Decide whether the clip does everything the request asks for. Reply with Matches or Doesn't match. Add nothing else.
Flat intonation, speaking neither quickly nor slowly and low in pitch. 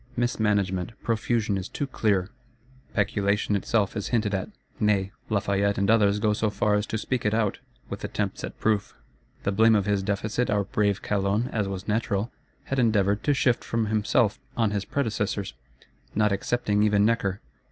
Matches